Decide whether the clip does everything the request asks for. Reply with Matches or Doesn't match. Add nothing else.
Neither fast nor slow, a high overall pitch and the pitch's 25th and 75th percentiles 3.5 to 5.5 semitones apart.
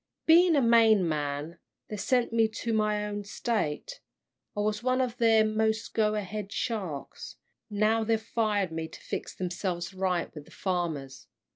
Matches